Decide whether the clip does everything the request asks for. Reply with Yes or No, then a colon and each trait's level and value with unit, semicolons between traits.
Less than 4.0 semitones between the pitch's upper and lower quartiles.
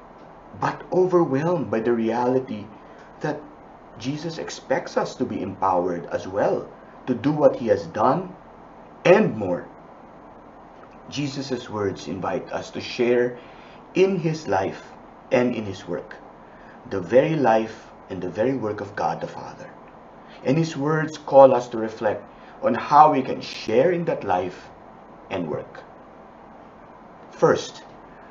No: wide, 5.6 semitones